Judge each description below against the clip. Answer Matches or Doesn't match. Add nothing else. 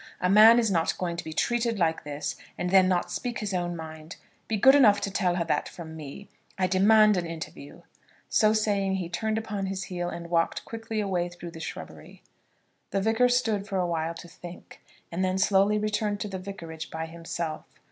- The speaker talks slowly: Doesn't match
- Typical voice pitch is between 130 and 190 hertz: Matches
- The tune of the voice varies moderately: Matches